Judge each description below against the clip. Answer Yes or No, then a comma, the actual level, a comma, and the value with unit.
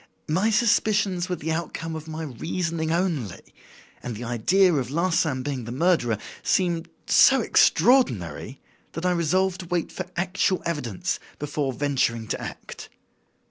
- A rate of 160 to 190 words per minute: No, average, 140 wpm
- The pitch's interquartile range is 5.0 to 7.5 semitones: Yes, wide, 5.6 semitones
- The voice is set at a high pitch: No, medium, 160 Hz